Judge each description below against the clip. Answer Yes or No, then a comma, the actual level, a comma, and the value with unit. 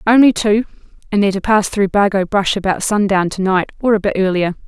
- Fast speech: Yes, fast, 220 wpm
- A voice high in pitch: Yes, high, 200 Hz